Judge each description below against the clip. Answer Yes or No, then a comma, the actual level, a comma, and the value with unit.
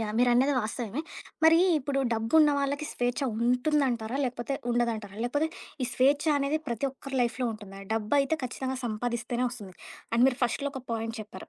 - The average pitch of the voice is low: No, high, 245 Hz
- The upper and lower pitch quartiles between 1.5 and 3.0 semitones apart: No, average, 3.5 semitones